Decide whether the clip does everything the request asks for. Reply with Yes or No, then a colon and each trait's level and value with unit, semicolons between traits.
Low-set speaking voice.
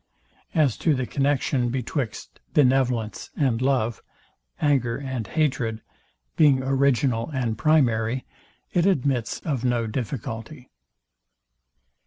Yes: low, 130 Hz